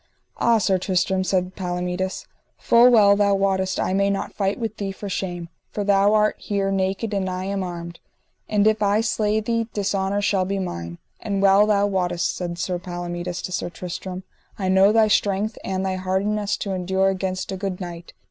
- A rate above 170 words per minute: Yes, average, 190 wpm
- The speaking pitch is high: Yes, high, 195 Hz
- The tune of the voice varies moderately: No, narrow, 1.8 semitones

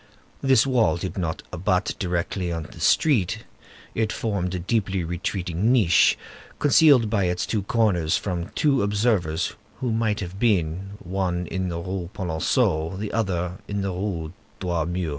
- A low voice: Yes, very low, 95 Hz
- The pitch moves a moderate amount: Yes, average, 3.4 semitones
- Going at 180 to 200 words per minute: No, average, 155 wpm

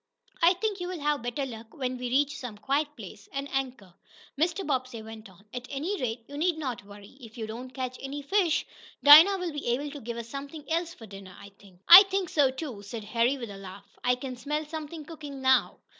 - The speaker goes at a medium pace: No, fast, 220 wpm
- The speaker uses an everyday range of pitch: Yes, average, 4.7 semitones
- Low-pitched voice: No, very high, 265 Hz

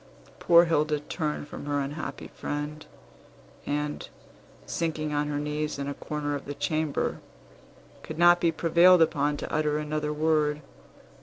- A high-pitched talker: No, medium, 150 Hz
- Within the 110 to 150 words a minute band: Yes, average, 145 wpm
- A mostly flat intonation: Yes, narrow, 1.2 semitones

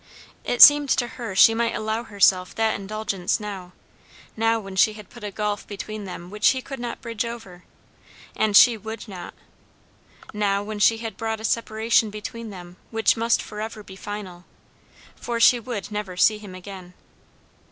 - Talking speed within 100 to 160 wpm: No, average, 175 wpm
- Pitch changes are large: No, narrow, 2.4 semitones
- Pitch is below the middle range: No, high, 215 Hz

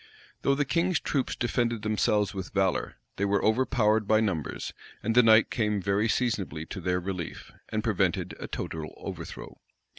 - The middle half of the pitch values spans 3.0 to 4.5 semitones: Yes, average, 3.4 semitones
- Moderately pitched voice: No, low, 105 Hz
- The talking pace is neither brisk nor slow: Yes, average, 160 wpm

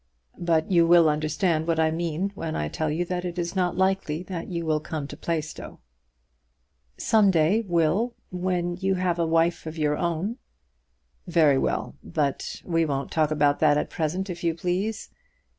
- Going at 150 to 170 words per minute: No, average, 180 wpm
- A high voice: No, medium, 170 Hz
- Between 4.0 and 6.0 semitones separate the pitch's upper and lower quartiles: No, narrow, 2.6 semitones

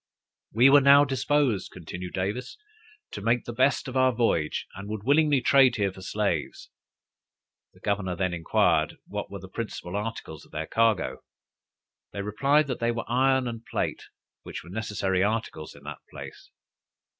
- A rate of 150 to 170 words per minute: Yes, average, 165 wpm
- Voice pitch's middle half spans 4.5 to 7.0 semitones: Yes, wide, 5.4 semitones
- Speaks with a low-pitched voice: Yes, low, 110 Hz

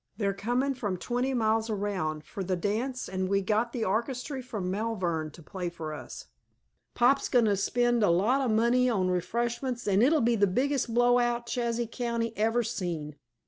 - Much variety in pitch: No, average, 4.2 semitones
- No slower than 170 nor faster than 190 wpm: Yes, average, 185 wpm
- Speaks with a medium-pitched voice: No, high, 225 Hz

